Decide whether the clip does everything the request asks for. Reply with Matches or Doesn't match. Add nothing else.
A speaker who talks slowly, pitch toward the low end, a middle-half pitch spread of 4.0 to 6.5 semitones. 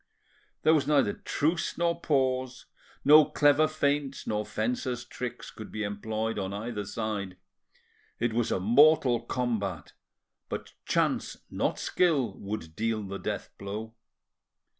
Matches